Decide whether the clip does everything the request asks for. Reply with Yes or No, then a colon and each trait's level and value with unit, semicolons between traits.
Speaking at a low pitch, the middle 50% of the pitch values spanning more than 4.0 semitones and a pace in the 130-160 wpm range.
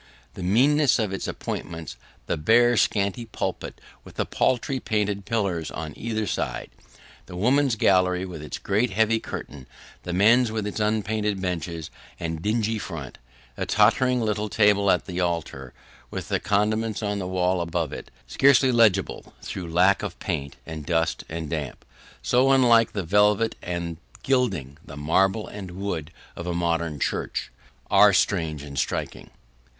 Yes: low, 100 Hz; average, 4.7 semitones; average, 155 wpm